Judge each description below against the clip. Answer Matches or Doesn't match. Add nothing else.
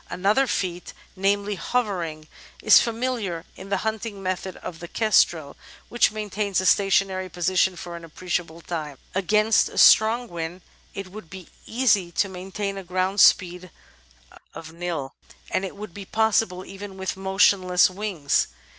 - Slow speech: Doesn't match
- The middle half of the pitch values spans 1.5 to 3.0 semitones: Matches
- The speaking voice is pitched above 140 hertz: Matches